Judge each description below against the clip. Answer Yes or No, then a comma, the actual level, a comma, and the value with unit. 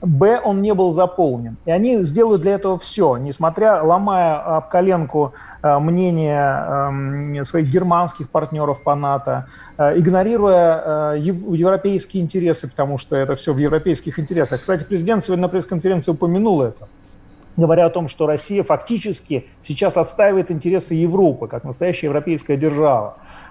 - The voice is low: No, medium, 165 Hz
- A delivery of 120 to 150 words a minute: Yes, average, 135 wpm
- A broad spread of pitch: No, average, 4.1 semitones